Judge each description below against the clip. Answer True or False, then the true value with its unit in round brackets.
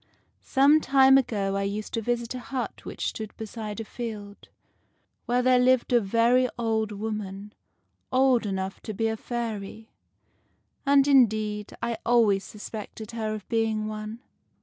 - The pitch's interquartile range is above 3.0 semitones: False (2.5 semitones)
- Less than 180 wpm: True (150 wpm)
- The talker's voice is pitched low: False (225 Hz)